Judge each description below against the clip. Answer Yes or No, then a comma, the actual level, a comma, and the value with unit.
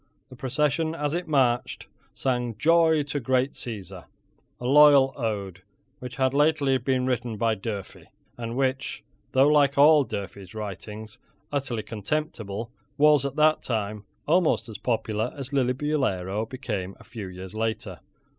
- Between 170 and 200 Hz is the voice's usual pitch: No, low, 125 Hz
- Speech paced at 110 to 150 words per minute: Yes, average, 140 wpm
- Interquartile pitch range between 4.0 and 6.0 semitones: Yes, average, 4.8 semitones